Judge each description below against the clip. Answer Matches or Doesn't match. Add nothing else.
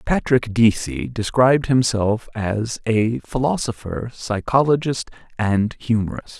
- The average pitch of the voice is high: Doesn't match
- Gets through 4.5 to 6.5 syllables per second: Doesn't match